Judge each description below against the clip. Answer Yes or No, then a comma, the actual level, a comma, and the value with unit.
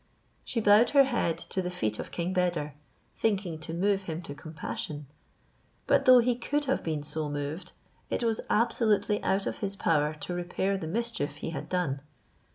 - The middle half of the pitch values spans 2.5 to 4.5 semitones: No, wide, 5.4 semitones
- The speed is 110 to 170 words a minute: No, average, 180 wpm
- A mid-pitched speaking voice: Yes, medium, 180 Hz